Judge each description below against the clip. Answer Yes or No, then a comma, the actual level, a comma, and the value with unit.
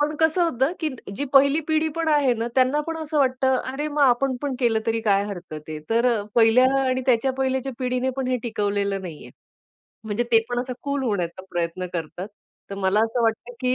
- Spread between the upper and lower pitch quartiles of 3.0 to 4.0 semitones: No, average, 4.4 semitones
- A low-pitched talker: No, very high, 250 Hz